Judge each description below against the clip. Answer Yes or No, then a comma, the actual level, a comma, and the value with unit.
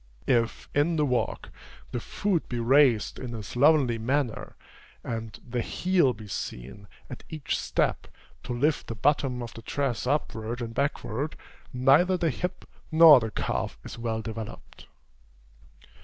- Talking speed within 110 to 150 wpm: Yes, average, 145 wpm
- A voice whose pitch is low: Yes, low, 125 Hz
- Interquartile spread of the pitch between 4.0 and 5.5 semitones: Yes, average, 4.4 semitones